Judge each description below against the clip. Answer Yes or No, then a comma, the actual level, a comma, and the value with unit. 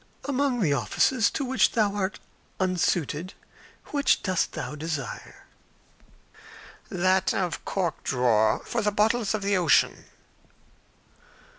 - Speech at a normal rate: No, slow, 115 wpm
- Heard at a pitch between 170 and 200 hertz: Yes, high, 190 Hz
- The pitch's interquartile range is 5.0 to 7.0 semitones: Yes, wide, 5.5 semitones